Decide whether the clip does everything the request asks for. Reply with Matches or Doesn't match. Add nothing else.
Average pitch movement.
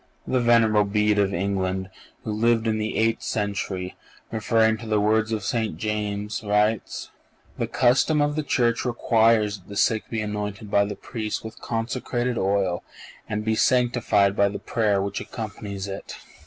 Doesn't match